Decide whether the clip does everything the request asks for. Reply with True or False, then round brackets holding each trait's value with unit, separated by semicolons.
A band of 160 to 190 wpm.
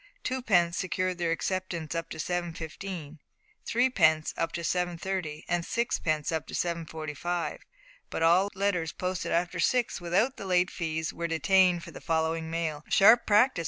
False (150 wpm)